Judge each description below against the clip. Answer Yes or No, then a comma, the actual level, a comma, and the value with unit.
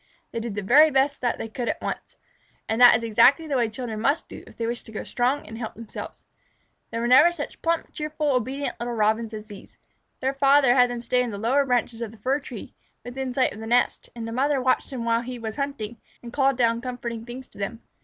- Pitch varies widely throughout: No, average, 2.9 semitones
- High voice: Yes, high, 245 Hz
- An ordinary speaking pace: No, fast, 245 wpm